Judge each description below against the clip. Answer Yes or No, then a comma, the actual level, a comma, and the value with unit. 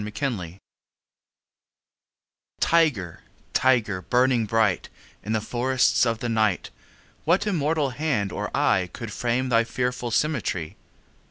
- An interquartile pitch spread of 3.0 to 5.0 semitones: Yes, average, 3.7 semitones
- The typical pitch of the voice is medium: No, low, 120 Hz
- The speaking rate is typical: No, slow, 115 wpm